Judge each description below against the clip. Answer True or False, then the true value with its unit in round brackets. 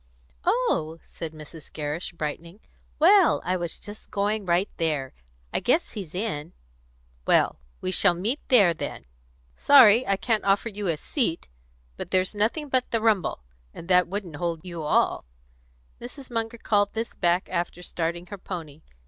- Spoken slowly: False (155 wpm)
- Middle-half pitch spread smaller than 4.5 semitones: False (4.9 semitones)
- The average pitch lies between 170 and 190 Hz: True (185 Hz)